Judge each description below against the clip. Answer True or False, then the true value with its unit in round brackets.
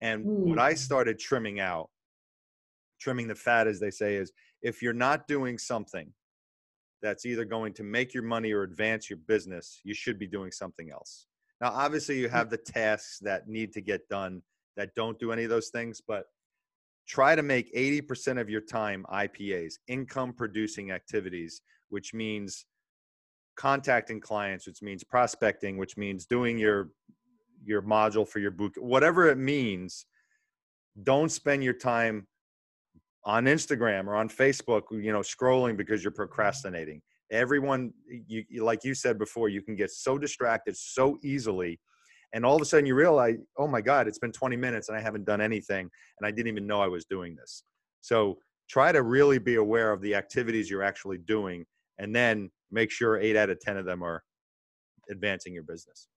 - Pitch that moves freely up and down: False (3.4 semitones)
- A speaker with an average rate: True (175 wpm)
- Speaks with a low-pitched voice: True (110 Hz)